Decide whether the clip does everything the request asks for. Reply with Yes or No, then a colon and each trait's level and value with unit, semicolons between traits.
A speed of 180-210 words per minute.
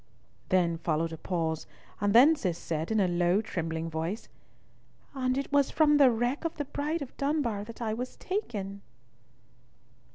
No: average, 165 wpm